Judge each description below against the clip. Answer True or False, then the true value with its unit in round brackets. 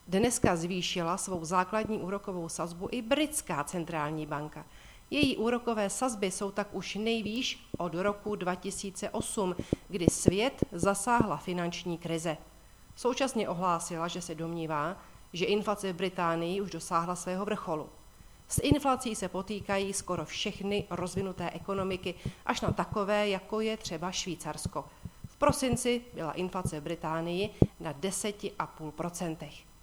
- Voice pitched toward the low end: False (185 Hz)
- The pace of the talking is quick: False (125 wpm)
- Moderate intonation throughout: True (3.5 semitones)